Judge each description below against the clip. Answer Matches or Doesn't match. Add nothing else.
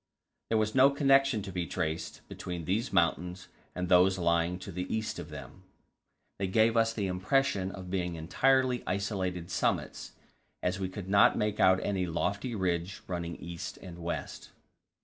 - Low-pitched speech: Matches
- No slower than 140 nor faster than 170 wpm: Matches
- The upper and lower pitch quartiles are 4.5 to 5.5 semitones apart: Doesn't match